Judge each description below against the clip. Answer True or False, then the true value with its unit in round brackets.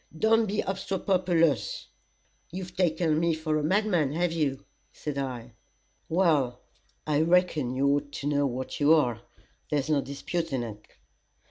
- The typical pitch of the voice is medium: True (155 Hz)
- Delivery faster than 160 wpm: False (145 wpm)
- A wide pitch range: False (4.3 semitones)